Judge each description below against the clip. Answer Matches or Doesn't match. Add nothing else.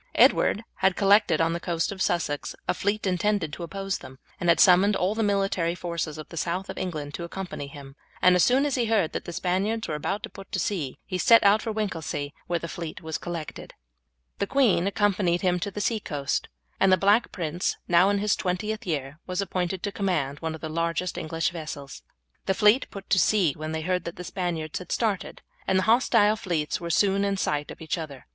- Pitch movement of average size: Matches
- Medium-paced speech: Doesn't match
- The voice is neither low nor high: Matches